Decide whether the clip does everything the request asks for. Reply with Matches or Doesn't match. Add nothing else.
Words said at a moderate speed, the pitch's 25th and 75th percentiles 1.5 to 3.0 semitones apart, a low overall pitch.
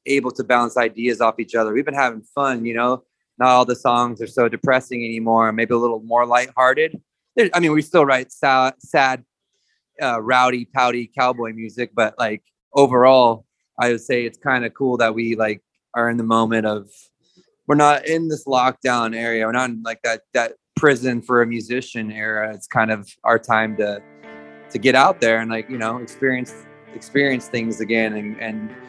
Matches